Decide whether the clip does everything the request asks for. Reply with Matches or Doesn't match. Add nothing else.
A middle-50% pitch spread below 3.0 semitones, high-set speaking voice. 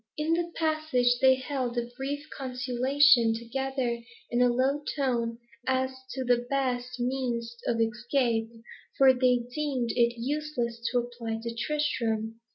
Matches